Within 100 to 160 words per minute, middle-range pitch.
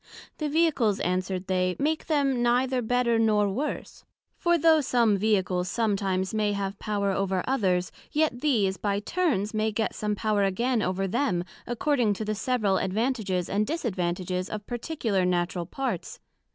No: average, 150 wpm; high, 210 Hz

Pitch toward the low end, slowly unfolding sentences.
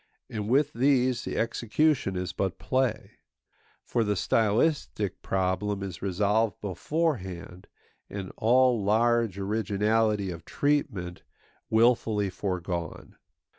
Yes: low, 105 Hz; slow, 100 wpm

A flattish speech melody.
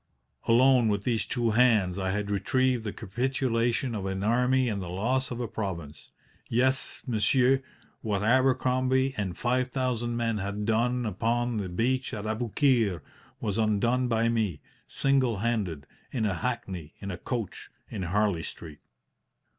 No: average, 3.7 semitones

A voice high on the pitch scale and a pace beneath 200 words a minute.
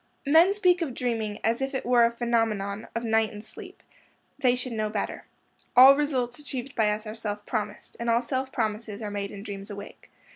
No: high, 230 Hz; fast, 205 wpm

